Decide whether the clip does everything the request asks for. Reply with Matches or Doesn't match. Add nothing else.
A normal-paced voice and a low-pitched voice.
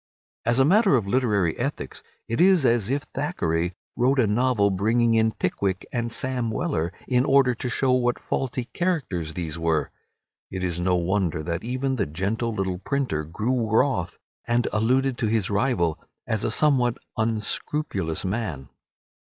Matches